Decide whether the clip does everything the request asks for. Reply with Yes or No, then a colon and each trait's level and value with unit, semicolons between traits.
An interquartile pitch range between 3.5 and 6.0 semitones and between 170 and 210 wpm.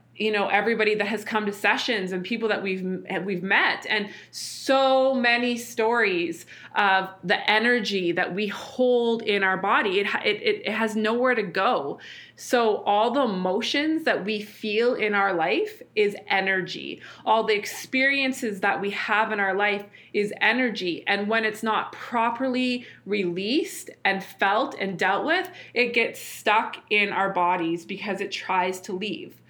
No: average, 3.8 semitones; average, 160 wpm